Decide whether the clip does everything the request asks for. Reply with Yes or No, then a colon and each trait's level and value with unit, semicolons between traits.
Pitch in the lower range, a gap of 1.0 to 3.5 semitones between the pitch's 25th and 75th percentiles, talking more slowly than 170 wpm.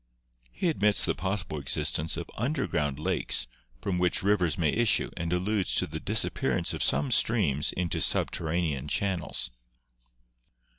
No: very low, 90 Hz; average, 5.2 semitones; average, 140 wpm